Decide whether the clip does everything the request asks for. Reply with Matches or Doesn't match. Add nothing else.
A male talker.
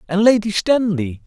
Matches